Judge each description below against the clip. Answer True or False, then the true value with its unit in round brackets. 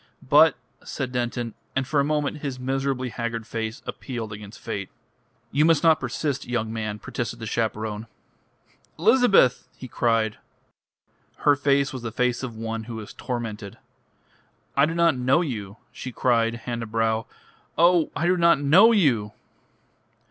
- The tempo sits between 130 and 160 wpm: True (155 wpm)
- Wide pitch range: False (4.1 semitones)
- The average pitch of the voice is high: False (125 Hz)